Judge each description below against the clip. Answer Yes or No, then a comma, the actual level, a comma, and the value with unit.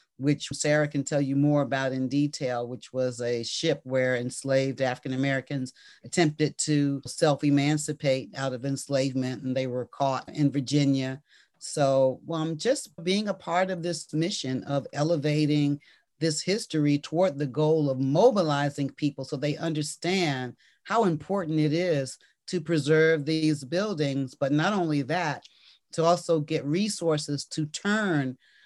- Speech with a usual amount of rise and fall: Yes, average, 3.1 semitones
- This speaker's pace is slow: No, average, 145 wpm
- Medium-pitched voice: Yes, medium, 145 Hz